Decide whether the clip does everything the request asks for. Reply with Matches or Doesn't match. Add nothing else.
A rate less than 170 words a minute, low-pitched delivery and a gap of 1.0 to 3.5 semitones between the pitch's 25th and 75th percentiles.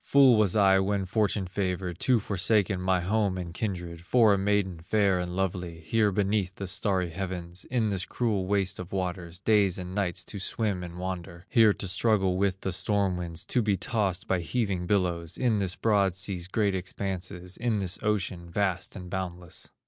Doesn't match